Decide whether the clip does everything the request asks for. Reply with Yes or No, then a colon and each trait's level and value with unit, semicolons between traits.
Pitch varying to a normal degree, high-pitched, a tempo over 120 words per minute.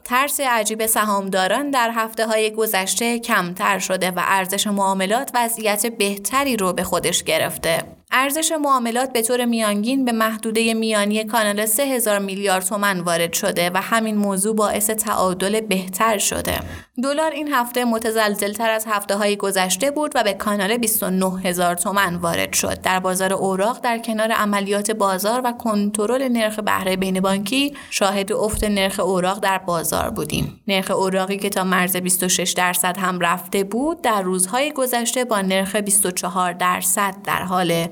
Yes: average, 3.3 semitones; high, 205 Hz; average, 150 wpm